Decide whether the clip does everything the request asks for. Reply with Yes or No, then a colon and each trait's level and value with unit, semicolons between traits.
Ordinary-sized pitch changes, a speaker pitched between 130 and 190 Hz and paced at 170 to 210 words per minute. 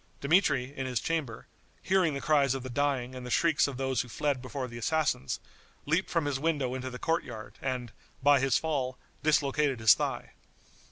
Yes: average, 3.0 semitones; low, 135 Hz; average, 190 wpm